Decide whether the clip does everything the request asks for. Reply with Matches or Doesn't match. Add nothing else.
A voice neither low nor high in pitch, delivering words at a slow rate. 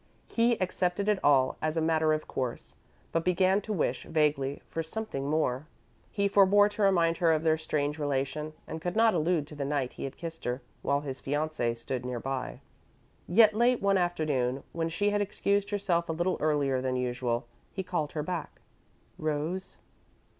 Doesn't match